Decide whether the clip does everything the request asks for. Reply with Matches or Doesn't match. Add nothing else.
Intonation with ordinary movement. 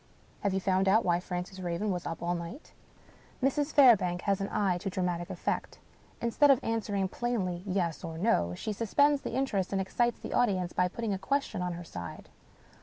Matches